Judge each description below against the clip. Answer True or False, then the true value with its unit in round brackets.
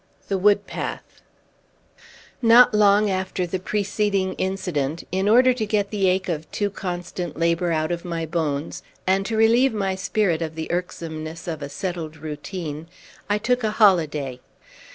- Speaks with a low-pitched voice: False (185 Hz)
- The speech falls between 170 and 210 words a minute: False (160 wpm)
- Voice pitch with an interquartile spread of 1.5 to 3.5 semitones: False (4.0 semitones)